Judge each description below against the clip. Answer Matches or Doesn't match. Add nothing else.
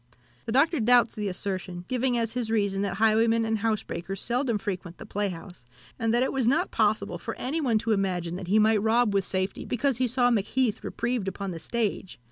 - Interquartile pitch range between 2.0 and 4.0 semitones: Matches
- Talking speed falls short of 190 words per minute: Doesn't match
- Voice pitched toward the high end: Matches